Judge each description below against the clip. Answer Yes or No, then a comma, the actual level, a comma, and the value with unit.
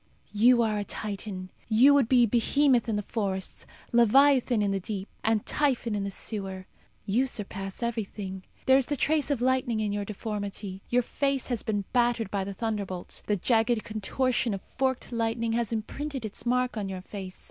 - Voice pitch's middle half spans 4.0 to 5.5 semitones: No, average, 3.6 semitones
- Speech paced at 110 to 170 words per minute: No, average, 185 wpm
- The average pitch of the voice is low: No, high, 225 Hz